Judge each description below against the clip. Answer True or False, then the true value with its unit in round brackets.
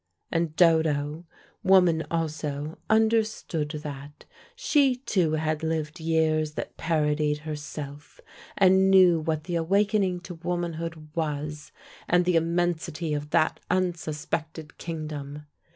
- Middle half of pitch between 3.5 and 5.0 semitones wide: False (2.7 semitones)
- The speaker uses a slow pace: True (110 wpm)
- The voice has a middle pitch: True (160 Hz)